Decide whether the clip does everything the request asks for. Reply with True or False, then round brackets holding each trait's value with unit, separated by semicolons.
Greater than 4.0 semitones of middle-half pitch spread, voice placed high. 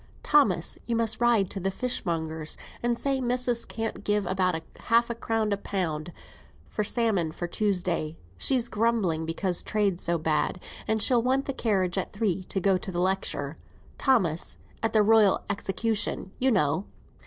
True (4.7 semitones; 200 Hz)